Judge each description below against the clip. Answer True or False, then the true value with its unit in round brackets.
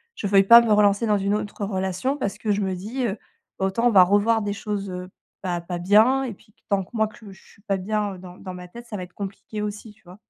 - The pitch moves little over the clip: True (2.3 semitones)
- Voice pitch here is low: False (200 Hz)